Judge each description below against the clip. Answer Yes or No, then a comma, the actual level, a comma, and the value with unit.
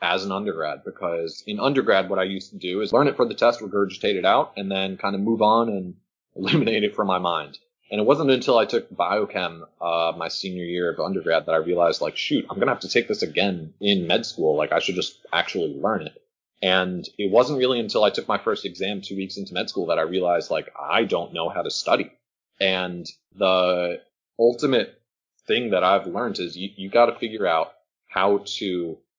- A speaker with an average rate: No, fast, 220 wpm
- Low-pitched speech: Yes, very low, 95 Hz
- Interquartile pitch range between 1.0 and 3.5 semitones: Yes, narrow, 2.5 semitones